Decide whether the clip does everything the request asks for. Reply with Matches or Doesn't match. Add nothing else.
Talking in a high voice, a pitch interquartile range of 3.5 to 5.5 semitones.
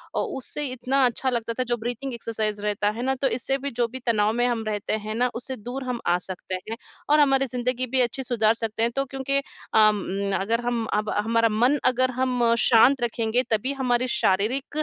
Doesn't match